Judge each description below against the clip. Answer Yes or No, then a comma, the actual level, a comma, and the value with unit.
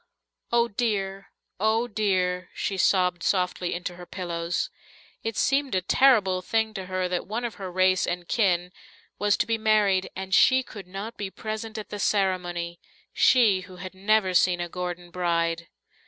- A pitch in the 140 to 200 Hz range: Yes, high, 190 Hz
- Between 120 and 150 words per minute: No, average, 170 wpm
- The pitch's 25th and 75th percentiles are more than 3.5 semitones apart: No, average, 3.1 semitones